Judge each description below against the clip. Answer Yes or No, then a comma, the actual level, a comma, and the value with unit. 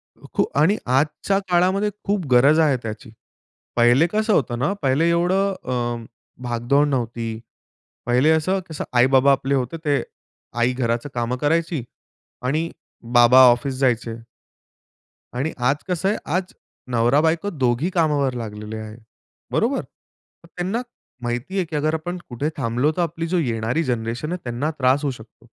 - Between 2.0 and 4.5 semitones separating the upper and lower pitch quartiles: No, wide, 5.4 semitones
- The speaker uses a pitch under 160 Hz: Yes, medium, 140 Hz